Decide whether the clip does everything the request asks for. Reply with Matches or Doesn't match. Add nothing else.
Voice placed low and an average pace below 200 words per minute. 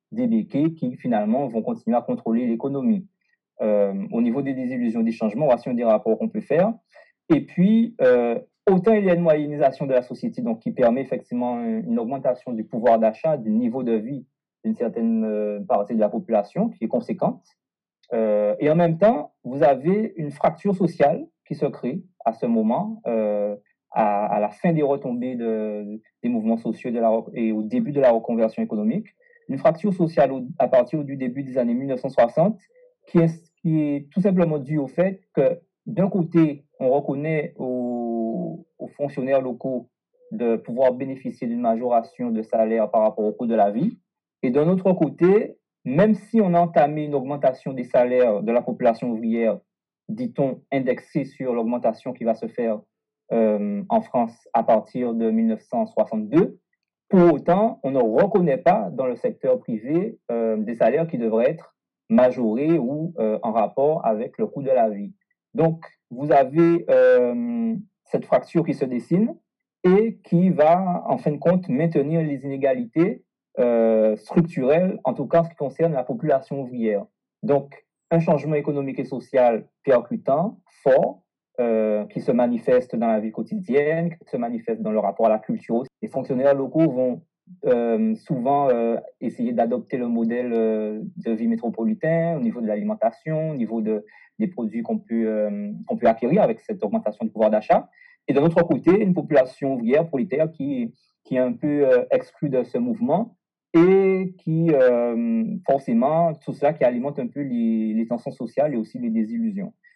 Doesn't match